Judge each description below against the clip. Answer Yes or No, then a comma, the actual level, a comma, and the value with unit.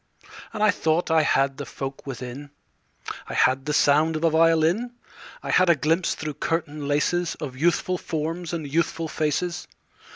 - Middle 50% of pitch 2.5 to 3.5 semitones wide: Yes, average, 2.8 semitones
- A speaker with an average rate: Yes, average, 165 wpm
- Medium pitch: Yes, medium, 160 Hz